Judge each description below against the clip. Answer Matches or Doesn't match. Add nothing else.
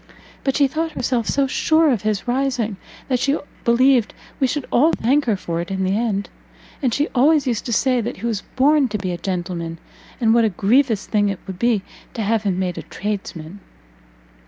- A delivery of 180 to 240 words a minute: Matches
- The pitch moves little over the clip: Doesn't match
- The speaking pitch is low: Doesn't match